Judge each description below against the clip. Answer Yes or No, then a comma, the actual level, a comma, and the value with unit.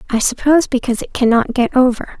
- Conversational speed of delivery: Yes, average, 190 wpm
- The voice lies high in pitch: Yes, very high, 250 Hz